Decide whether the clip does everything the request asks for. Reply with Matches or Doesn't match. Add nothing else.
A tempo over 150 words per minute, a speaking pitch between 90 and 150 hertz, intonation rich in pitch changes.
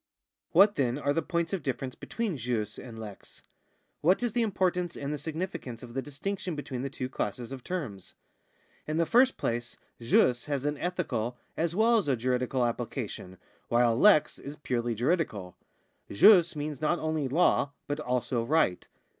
Matches